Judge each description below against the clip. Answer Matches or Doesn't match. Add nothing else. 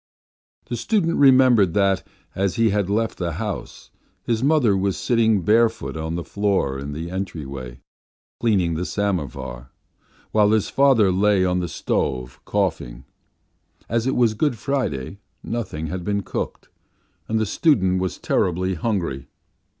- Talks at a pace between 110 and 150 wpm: Matches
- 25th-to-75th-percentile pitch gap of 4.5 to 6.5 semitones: Matches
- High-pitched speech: Doesn't match